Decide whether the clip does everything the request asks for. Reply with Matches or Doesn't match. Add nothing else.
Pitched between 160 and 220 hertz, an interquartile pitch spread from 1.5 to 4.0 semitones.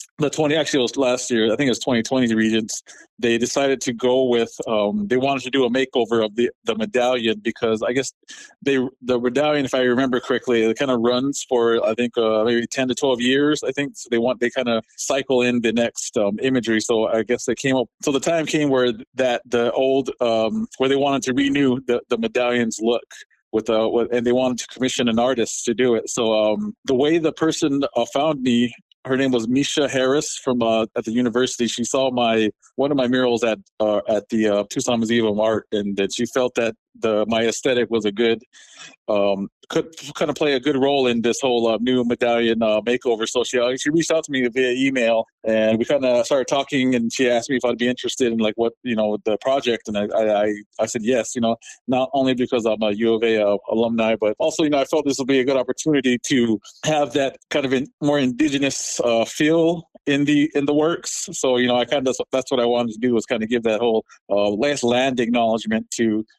Doesn't match